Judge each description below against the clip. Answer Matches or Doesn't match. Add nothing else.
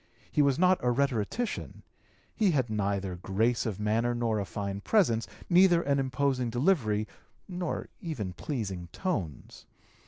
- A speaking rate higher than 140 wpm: Doesn't match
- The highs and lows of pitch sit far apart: Matches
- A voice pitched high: Doesn't match